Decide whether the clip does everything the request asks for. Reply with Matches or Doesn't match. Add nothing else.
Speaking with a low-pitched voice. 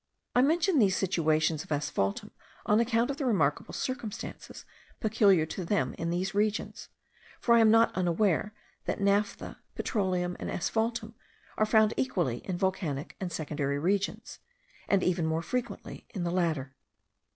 Doesn't match